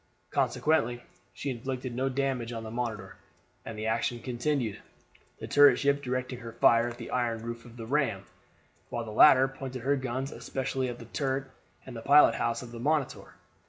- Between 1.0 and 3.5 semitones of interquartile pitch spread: Yes, narrow, 2.4 semitones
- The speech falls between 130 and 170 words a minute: No, average, 180 wpm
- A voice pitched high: No, low, 125 Hz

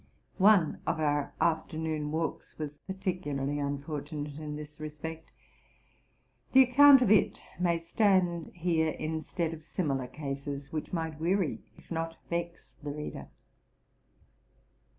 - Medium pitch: Yes, medium, 160 Hz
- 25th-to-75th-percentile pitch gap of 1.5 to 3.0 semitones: Yes, average, 2.7 semitones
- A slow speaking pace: Yes, slow, 120 wpm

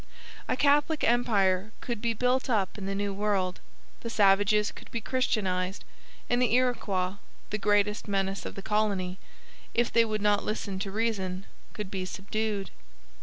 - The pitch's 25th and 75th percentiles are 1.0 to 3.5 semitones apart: Yes, average, 2.9 semitones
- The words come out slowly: No, average, 160 wpm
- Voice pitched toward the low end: No, high, 210 Hz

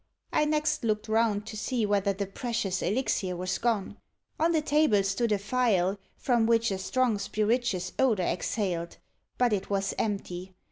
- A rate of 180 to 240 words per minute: No, average, 160 wpm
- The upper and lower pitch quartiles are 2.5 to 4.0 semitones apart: Yes, average, 3.7 semitones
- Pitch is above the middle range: Yes, high, 210 Hz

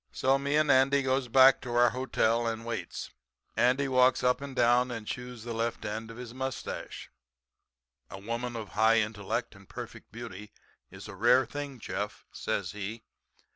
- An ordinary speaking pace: Yes, average, 175 wpm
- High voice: No, low, 120 Hz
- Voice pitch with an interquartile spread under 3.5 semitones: Yes, narrow, 2.6 semitones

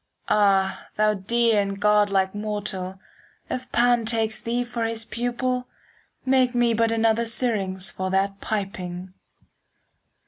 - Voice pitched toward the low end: No, high, 215 Hz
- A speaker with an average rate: No, slow, 130 wpm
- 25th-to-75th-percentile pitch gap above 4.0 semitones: No, average, 3.2 semitones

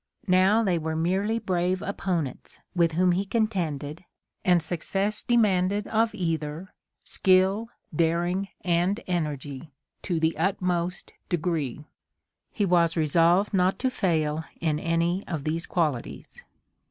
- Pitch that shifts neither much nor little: Yes, average, 3.0 semitones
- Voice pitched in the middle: Yes, medium, 175 Hz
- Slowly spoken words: Yes, slow, 120 wpm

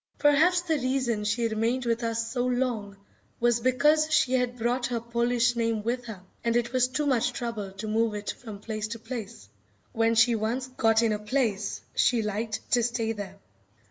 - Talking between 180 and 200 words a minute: Yes, average, 190 wpm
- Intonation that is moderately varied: No, narrow, 2.1 semitones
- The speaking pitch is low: No, high, 235 Hz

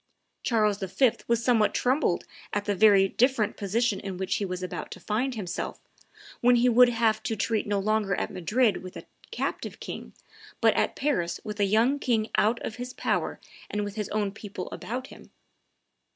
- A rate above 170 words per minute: Yes, average, 185 wpm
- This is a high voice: Yes, high, 215 Hz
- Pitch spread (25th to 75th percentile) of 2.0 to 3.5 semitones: Yes, average, 3.1 semitones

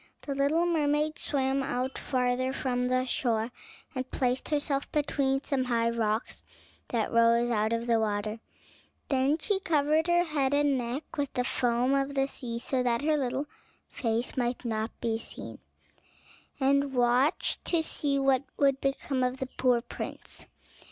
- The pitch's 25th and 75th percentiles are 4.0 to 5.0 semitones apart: No, average, 2.8 semitones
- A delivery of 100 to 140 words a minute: No, average, 160 wpm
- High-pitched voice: Yes, very high, 260 Hz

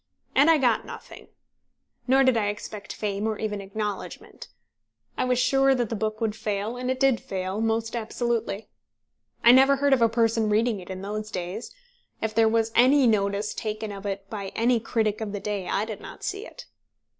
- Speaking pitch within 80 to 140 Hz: No, high, 220 Hz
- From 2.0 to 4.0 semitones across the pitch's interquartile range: Yes, average, 2.8 semitones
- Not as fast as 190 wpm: No, average, 195 wpm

